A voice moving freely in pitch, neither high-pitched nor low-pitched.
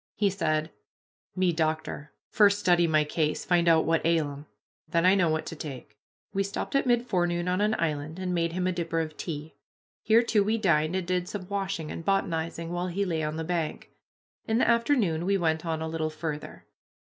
No: average, 3.4 semitones; medium, 170 Hz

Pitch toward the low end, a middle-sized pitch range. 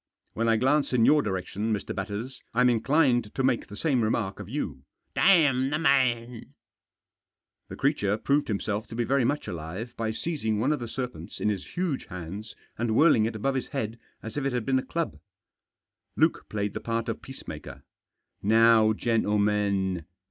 Yes: low, 115 Hz; average, 4.2 semitones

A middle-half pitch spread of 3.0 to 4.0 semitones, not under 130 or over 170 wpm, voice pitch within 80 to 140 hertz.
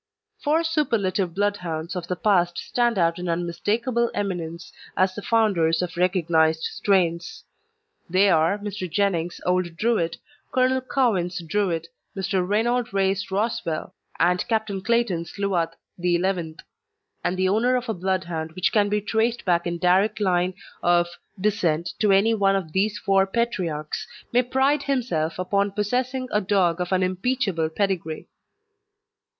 No: average, 3.7 semitones; average, 140 wpm; high, 190 Hz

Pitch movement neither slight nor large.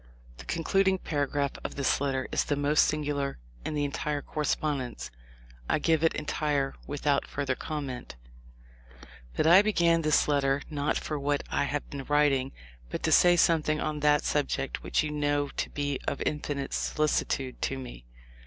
No: narrow, 1.6 semitones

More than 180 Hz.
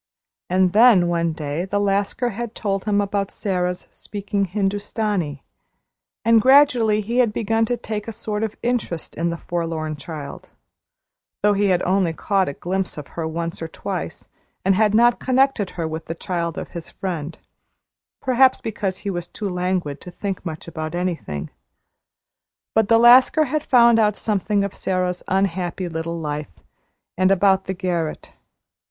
Yes: high, 190 Hz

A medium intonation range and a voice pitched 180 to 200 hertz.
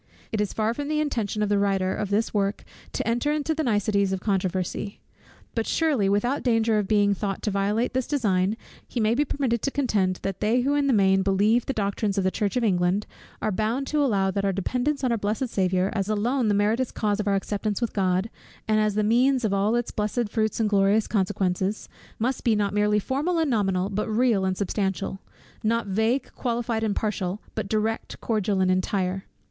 No: average, 3.2 semitones; high, 210 Hz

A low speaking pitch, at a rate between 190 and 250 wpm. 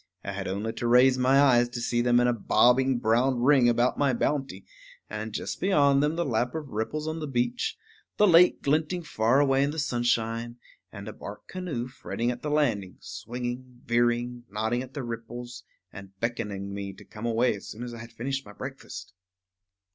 Yes: low, 120 Hz; average, 195 wpm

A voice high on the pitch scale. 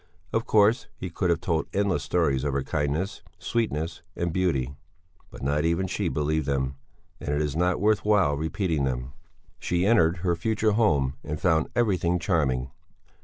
No: very low, 85 Hz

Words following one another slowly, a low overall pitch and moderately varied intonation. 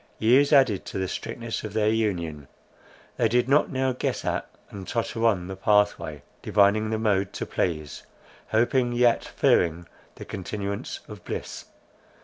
No: average, 150 wpm; low, 110 Hz; average, 3.6 semitones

